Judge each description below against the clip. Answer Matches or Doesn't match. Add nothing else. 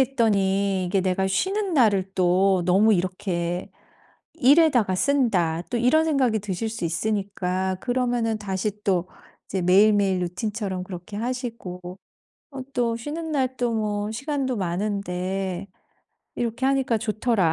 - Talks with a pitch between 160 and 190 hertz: Doesn't match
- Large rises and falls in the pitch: Doesn't match